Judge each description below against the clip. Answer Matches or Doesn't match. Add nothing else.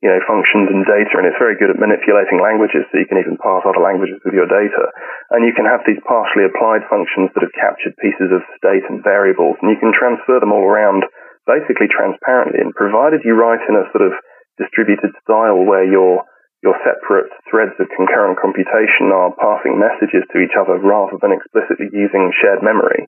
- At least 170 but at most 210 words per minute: Matches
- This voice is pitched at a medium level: Doesn't match